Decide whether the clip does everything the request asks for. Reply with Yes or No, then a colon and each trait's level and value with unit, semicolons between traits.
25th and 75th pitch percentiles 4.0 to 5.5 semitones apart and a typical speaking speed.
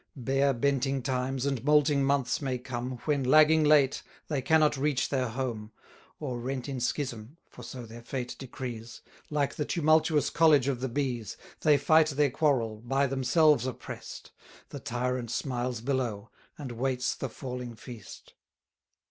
No: average, 2.8 semitones; average, 150 wpm